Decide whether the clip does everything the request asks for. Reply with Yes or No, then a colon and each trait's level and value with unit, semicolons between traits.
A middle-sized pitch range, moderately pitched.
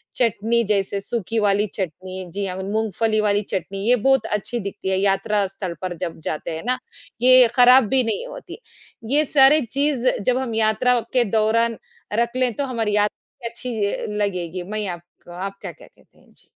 No: average, 3.8 semitones; high, 215 Hz